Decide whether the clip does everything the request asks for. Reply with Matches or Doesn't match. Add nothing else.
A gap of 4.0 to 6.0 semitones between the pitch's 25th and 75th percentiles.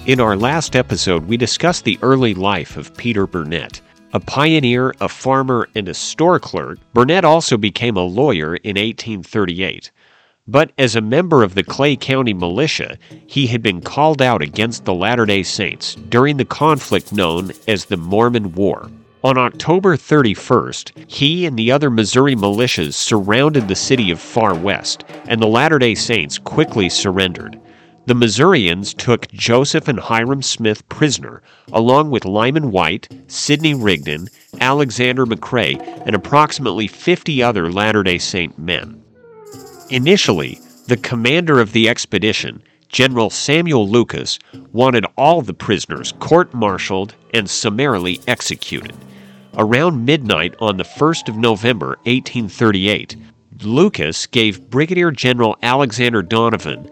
Matches